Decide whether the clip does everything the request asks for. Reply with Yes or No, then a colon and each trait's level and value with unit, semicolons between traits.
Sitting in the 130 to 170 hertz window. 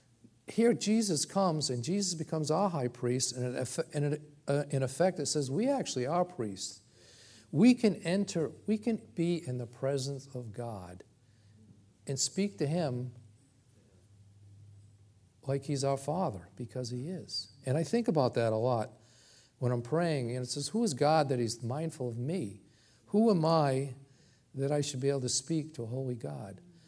Yes: low, 135 Hz